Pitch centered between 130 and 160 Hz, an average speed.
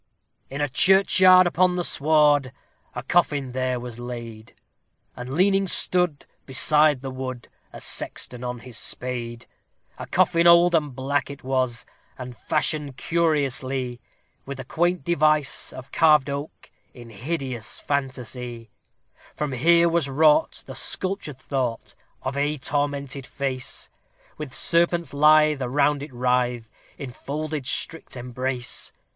No: medium, 140 Hz; slow, 130 wpm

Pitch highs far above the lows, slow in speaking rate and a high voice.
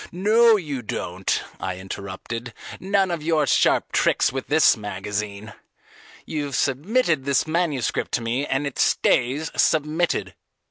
No: wide, 6.2 semitones; slow, 130 wpm; medium, 140 Hz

